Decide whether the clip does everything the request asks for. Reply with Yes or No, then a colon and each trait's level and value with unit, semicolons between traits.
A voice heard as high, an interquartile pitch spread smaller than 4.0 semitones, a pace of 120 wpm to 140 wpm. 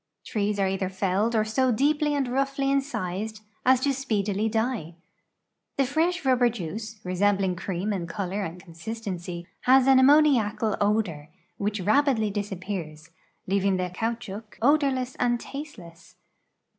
No: high, 215 Hz; wide, 5.4 semitones; slow, 135 wpm